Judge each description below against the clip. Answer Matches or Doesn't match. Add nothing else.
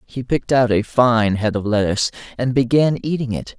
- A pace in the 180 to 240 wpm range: Matches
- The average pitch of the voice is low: Matches